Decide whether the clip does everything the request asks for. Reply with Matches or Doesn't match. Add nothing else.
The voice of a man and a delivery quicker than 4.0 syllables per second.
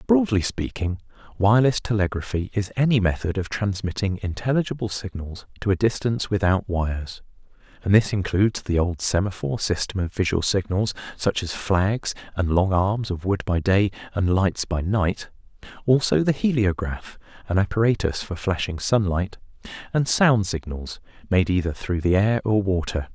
Matches